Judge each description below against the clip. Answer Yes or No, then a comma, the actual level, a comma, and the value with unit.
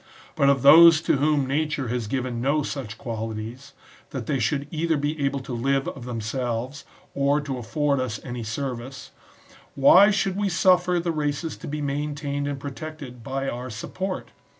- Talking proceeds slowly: No, average, 175 wpm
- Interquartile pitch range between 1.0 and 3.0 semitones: No, average, 3.4 semitones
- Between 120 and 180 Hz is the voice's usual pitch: Yes, medium, 140 Hz